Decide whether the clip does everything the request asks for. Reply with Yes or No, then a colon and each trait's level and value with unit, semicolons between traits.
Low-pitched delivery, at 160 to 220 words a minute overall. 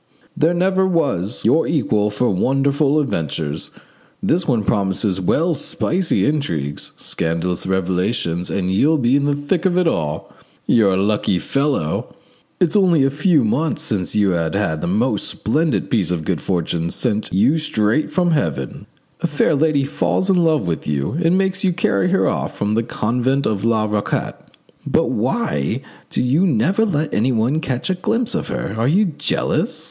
Yes: low, 125 Hz; average, 170 wpm